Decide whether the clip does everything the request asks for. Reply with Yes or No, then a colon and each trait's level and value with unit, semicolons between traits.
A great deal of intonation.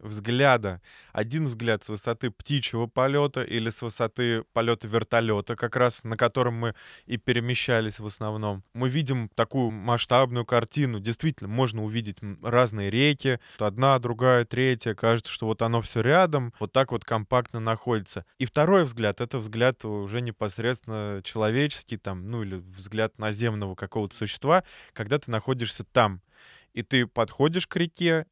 No: average, 2.8 semitones